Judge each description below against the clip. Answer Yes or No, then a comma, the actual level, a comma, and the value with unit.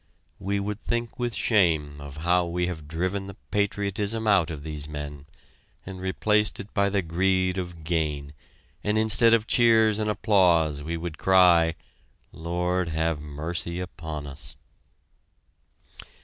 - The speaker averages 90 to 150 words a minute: Yes, average, 140 wpm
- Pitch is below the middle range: Yes, very low, 90 Hz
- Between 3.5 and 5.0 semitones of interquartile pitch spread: Yes, average, 4.2 semitones